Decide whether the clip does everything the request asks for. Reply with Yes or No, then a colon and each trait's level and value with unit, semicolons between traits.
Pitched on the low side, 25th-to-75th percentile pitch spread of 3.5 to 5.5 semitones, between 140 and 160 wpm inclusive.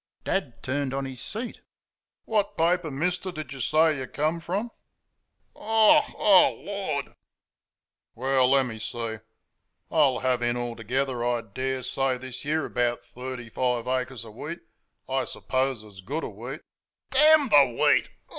Yes: low, 130 Hz; average, 4.7 semitones; average, 150 wpm